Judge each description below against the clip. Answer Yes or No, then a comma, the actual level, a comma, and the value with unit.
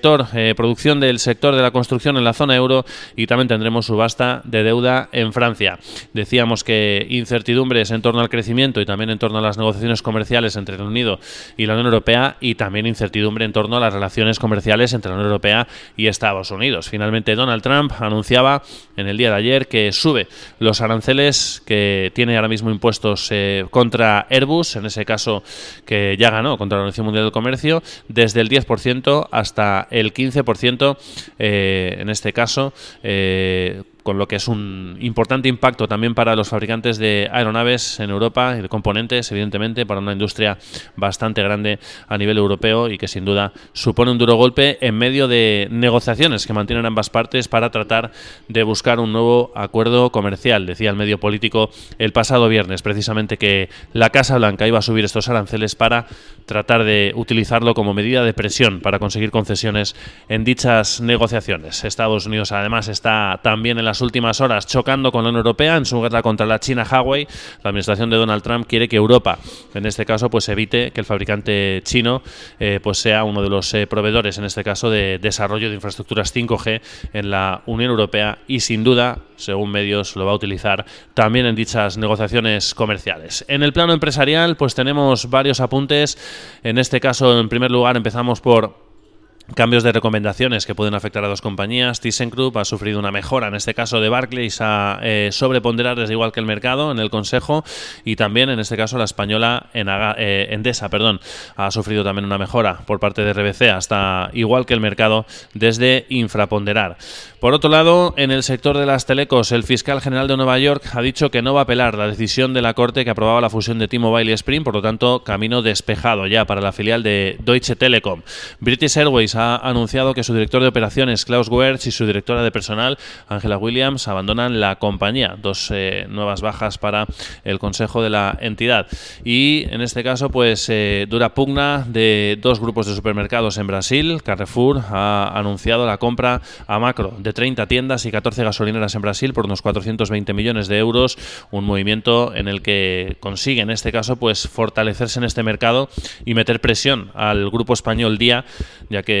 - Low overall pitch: Yes, low, 115 Hz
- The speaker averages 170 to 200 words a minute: Yes, fast, 190 wpm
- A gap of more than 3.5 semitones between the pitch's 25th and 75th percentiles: No, average, 2.8 semitones